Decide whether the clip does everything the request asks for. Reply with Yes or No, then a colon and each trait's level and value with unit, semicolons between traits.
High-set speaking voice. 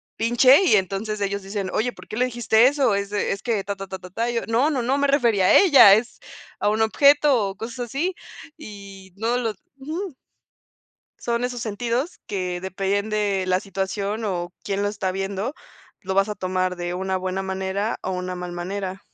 Yes: high, 205 Hz